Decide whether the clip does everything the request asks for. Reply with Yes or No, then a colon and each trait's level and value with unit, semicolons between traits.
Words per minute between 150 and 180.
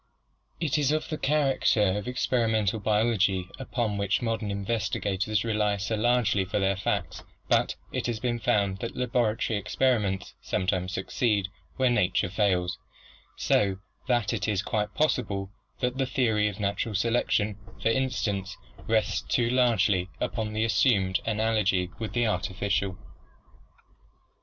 No: average, 140 wpm